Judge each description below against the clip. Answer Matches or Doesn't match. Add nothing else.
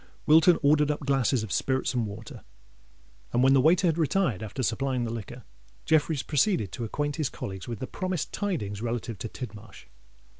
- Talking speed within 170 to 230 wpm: Matches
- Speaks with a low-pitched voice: Matches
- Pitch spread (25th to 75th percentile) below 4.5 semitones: Doesn't match